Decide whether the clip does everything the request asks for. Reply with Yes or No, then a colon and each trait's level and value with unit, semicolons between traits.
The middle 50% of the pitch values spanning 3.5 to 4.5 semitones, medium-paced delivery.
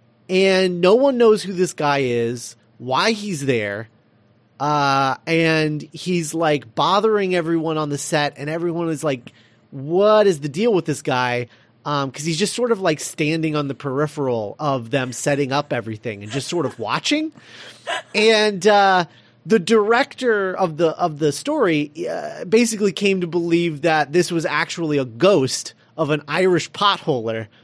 No: wide, 5.5 semitones; average, 165 wpm